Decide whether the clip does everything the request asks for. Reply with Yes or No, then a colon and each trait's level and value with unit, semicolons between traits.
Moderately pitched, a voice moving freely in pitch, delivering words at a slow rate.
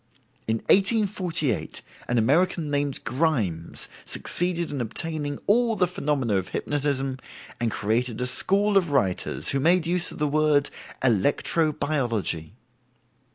Yes: medium, 145 Hz; wide, 6.1 semitones; slow, 125 wpm